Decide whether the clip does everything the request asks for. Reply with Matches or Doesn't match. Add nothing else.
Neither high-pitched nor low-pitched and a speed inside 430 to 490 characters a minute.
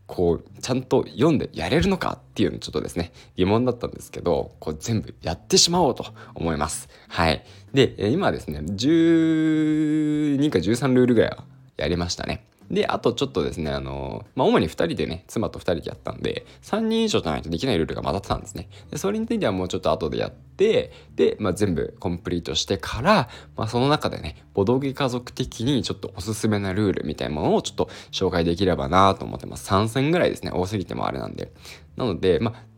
Doesn't match